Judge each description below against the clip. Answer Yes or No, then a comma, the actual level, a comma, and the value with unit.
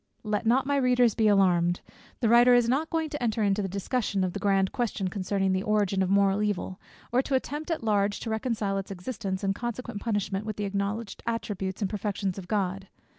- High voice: Yes, high, 205 Hz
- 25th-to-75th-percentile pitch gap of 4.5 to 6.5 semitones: No, average, 3.2 semitones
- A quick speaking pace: Yes, fast, 210 wpm